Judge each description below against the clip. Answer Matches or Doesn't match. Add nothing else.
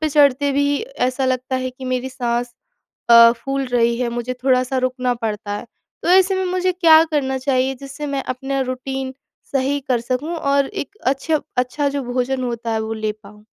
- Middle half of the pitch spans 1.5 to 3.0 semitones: Matches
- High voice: Matches